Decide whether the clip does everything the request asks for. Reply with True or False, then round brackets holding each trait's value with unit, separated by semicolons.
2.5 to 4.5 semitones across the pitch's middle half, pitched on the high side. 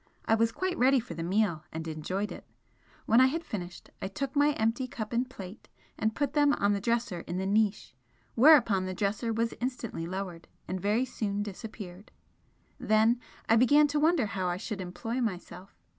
False (4.9 semitones; 215 Hz)